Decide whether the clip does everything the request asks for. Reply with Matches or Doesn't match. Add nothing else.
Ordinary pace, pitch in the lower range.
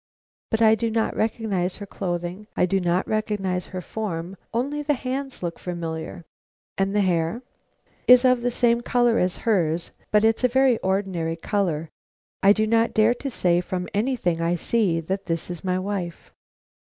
Doesn't match